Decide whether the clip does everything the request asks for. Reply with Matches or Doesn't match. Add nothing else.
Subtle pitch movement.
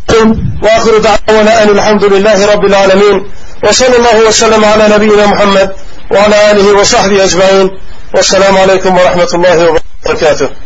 Matches